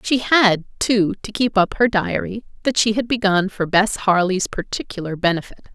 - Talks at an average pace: Yes, average, 180 wpm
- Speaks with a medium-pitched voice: No, high, 205 Hz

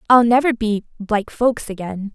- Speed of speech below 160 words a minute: Yes, average, 140 wpm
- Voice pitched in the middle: No, high, 220 Hz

